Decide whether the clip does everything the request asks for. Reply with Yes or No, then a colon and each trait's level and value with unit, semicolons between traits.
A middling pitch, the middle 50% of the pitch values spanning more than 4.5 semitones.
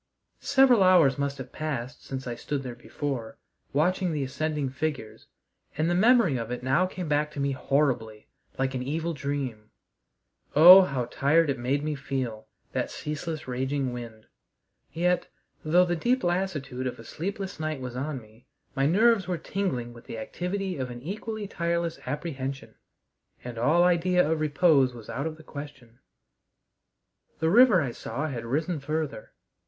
Yes: medium, 145 Hz; average, 5.0 semitones